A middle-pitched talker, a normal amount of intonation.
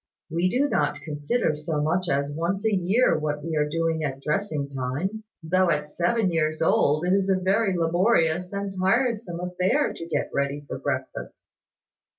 Yes: medium, 170 Hz; average, 4.3 semitones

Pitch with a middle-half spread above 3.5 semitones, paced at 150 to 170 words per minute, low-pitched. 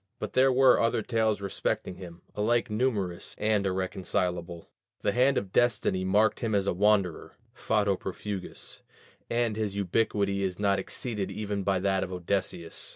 No: average, 2.8 semitones; average, 155 wpm; low, 100 Hz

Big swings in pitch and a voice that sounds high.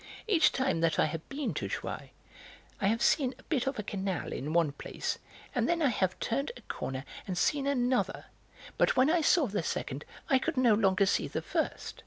Yes: wide, 7.5 semitones; high, 230 Hz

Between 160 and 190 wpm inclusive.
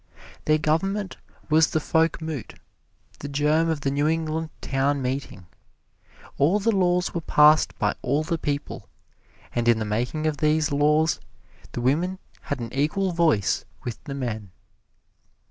No: average, 145 wpm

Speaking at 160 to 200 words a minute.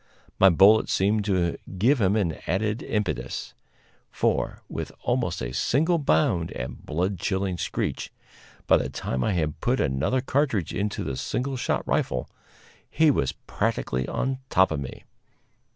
No: average, 150 wpm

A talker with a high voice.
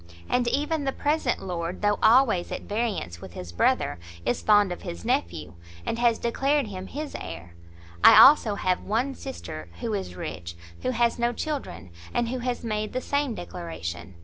Yes: high, 215 Hz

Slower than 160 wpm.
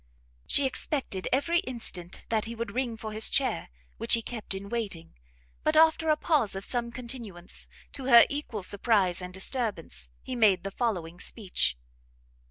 No: average, 165 wpm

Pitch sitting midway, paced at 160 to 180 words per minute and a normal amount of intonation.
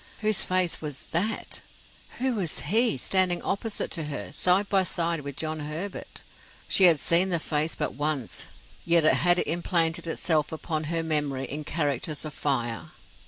Yes: medium, 165 Hz; average, 165 wpm; average, 3.4 semitones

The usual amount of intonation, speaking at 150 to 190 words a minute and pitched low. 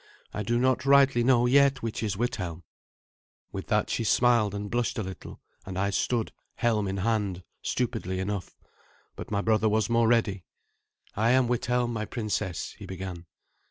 Yes: average, 3.5 semitones; average, 170 wpm; low, 110 Hz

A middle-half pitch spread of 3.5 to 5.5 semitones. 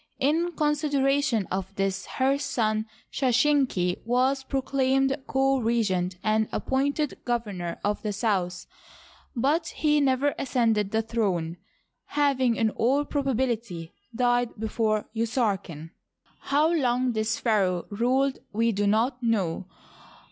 Yes: average, 4.5 semitones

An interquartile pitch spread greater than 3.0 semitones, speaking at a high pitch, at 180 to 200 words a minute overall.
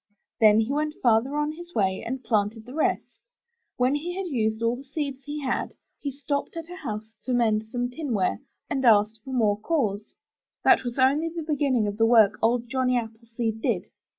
Yes: average, 4.6 semitones; high, 245 Hz; average, 195 wpm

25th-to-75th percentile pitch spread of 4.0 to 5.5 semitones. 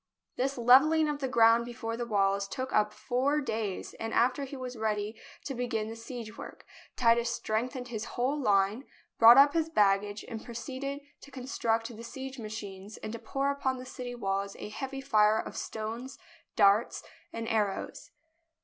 No: average, 3.4 semitones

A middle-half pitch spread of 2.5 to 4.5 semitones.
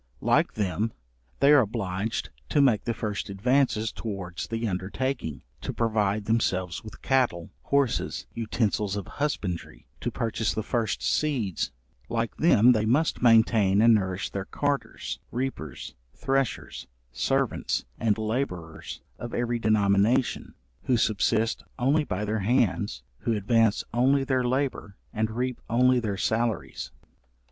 Yes: average, 3.8 semitones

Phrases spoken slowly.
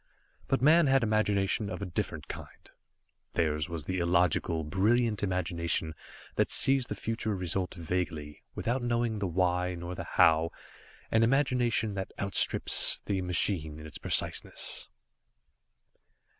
Yes: slow, 130 wpm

